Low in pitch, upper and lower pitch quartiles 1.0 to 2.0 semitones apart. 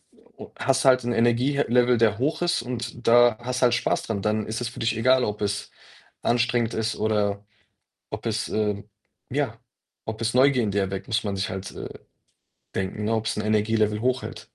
No: low, 115 Hz; narrow, 2.5 semitones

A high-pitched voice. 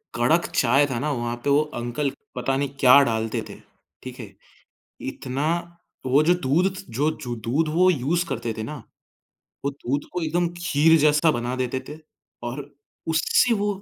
No: medium, 140 Hz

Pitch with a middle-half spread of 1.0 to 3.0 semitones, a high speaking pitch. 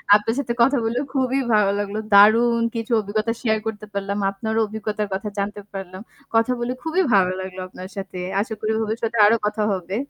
Yes: narrow, 2.4 semitones; high, 215 Hz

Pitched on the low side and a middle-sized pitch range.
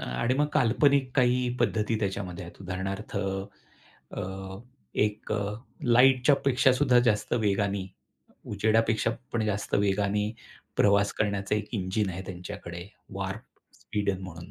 Yes: low, 105 Hz; average, 3.3 semitones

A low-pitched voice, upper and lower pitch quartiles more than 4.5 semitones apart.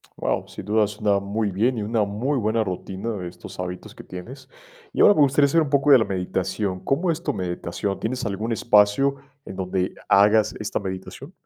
Yes: low, 105 Hz; average, 5.2 semitones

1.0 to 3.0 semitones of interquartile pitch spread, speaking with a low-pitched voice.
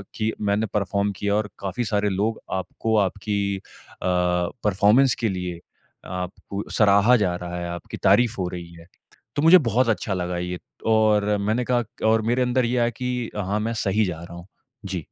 No: average, 3.7 semitones; low, 105 Hz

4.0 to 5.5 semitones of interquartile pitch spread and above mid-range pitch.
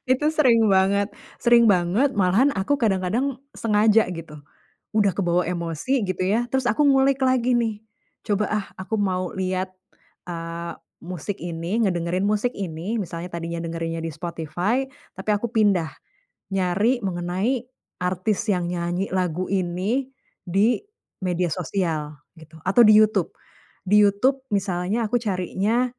Yes: average, 4.3 semitones; high, 195 Hz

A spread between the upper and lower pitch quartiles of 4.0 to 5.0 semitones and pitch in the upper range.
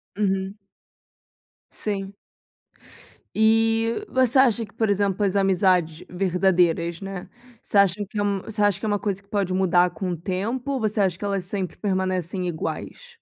No: narrow, 2.5 semitones; high, 195 Hz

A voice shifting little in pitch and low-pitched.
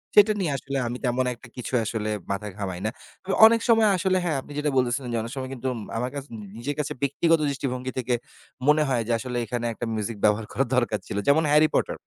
No: average, 4.1 semitones; low, 130 Hz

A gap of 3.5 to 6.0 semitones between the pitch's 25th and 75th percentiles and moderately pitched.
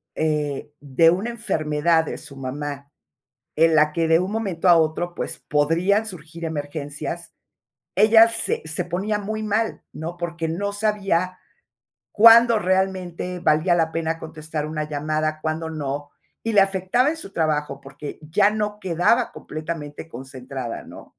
Yes: average, 4.3 semitones; medium, 165 Hz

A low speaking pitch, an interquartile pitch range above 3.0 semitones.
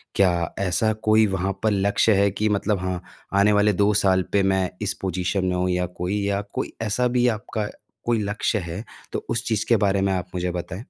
No: low, 100 Hz; narrow, 2.5 semitones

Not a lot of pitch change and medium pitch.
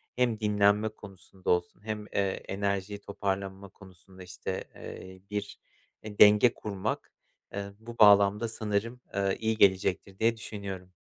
No: narrow, 1.8 semitones; low, 100 Hz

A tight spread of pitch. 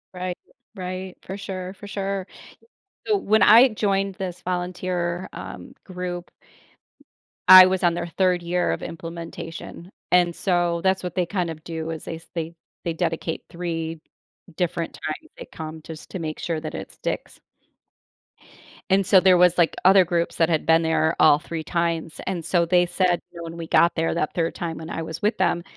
Yes: narrow, 2.0 semitones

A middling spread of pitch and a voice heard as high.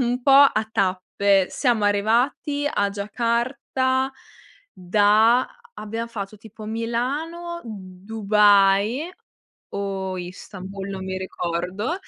Yes: average, 3.7 semitones; high, 210 Hz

